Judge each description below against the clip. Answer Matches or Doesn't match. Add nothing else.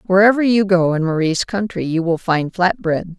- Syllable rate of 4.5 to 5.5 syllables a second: Matches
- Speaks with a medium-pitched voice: Matches